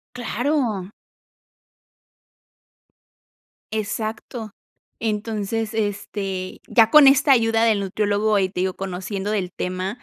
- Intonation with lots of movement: No, narrow, 2.6 semitones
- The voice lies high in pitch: Yes, high, 210 Hz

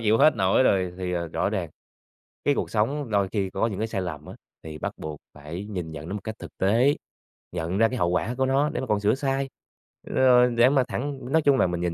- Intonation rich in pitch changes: Yes, wide, 6.5 semitones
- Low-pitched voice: Yes, low, 105 Hz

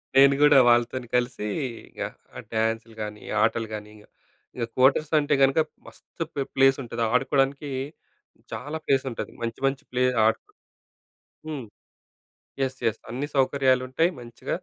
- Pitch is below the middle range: Yes, low, 130 Hz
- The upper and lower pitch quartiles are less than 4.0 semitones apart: Yes, average, 3.1 semitones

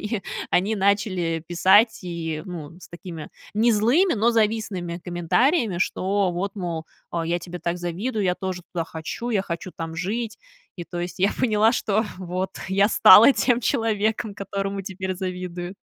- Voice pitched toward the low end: No, high, 190 Hz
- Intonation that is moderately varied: Yes, average, 3.5 semitones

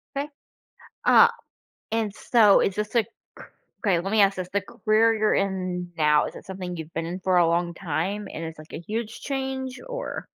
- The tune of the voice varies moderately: Yes, average, 3.9 semitones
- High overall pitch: Yes, high, 195 Hz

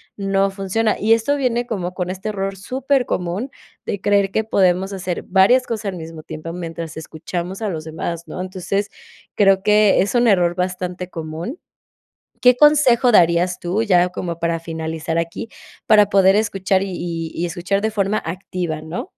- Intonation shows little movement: No, average, 3.6 semitones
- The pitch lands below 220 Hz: Yes, high, 190 Hz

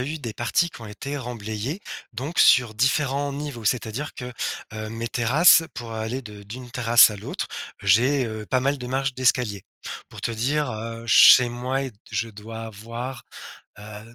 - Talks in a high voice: No, low, 120 Hz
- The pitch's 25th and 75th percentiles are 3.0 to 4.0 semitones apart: Yes, average, 3.3 semitones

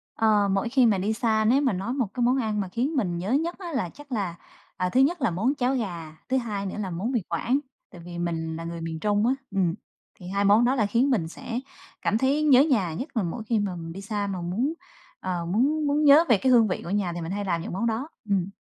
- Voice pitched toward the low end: No, high, 215 Hz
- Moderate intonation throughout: No, wide, 5.8 semitones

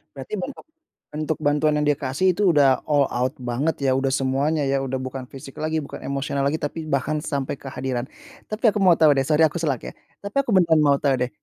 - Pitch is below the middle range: No, medium, 145 Hz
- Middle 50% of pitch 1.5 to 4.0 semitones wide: Yes, average, 2.8 semitones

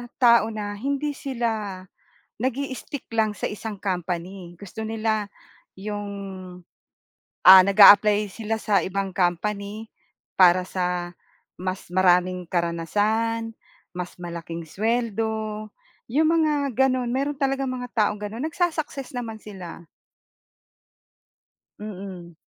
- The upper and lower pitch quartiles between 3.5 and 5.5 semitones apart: Yes, average, 4.1 semitones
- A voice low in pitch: No, high, 210 Hz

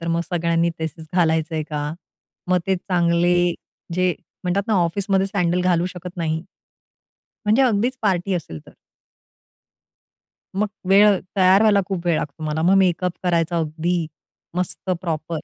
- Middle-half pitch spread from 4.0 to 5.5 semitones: No, narrow, 2.4 semitones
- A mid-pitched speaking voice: Yes, medium, 175 Hz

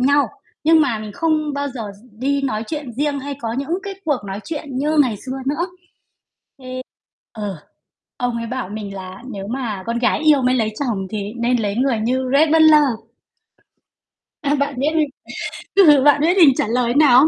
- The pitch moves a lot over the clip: No, average, 4.6 semitones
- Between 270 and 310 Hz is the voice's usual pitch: No, very high, 260 Hz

